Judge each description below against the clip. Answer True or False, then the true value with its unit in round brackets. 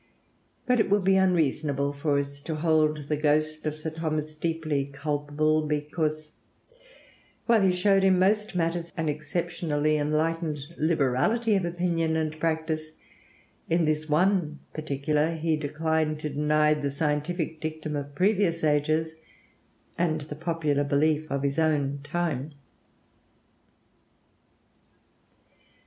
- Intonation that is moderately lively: False (1.9 semitones)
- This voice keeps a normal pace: False (125 wpm)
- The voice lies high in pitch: False (155 Hz)